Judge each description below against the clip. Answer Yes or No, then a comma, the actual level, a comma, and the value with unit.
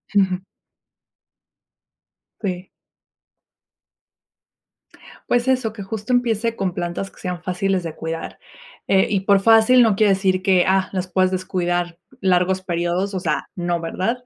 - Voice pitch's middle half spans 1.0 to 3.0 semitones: Yes, narrow, 2.6 semitones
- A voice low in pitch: No, high, 190 Hz